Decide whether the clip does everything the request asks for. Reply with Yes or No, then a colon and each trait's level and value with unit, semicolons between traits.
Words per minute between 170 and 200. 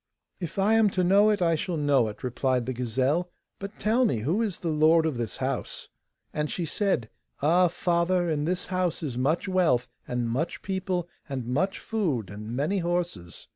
Yes: average, 190 wpm